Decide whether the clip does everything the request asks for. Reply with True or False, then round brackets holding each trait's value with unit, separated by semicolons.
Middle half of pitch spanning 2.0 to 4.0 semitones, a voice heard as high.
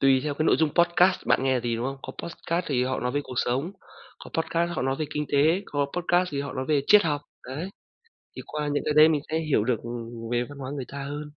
False (3.5 semitones; 145 Hz)